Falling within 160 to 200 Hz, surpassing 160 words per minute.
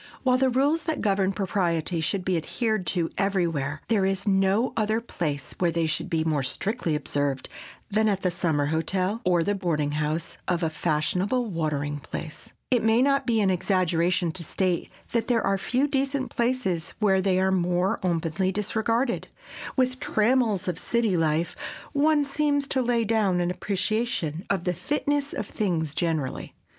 Yes: high, 190 Hz; average, 170 wpm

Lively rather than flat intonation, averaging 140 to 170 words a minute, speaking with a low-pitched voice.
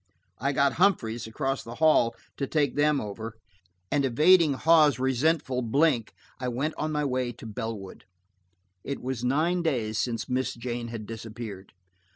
No: average, 4.4 semitones; average, 155 wpm; low, 130 Hz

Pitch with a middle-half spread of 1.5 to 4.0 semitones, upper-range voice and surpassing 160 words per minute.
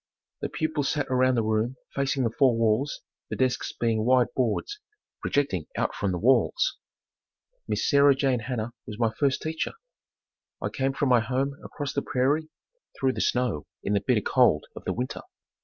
No: average, 3.4 semitones; low, 130 Hz; average, 175 wpm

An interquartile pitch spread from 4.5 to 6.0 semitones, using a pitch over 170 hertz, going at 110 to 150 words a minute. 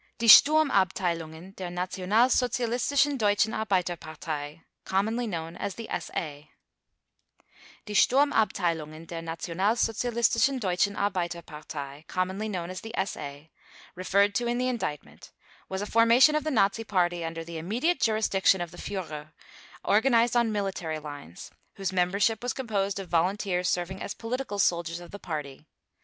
Yes: average, 5.1 semitones; high, 190 Hz; slow, 135 wpm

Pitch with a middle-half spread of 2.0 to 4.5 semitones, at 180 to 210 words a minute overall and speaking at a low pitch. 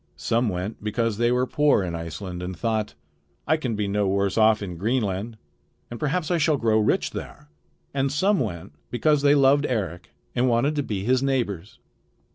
No: average, 5.3 semitones; average, 185 wpm; low, 115 Hz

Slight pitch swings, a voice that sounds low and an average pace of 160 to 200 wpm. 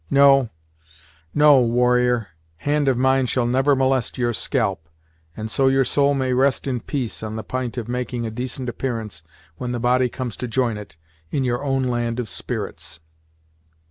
Yes: narrow, 2.1 semitones; low, 125 Hz; average, 175 wpm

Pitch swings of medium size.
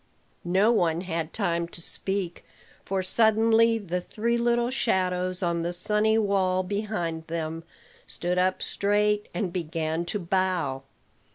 Yes: average, 3.6 semitones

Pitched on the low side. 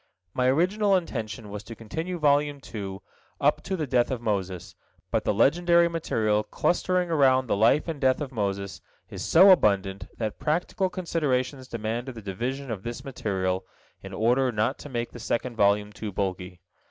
Yes: low, 120 Hz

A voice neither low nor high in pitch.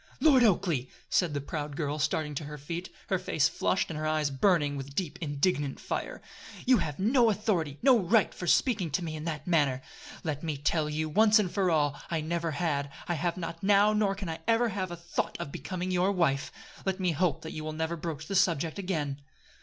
Yes: medium, 165 Hz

